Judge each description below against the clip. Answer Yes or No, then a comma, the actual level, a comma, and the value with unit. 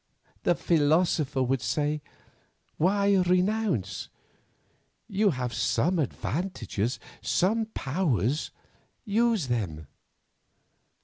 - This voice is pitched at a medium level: Yes, medium, 160 Hz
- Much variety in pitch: Yes, wide, 7.2 semitones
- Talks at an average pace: No, slow, 75 wpm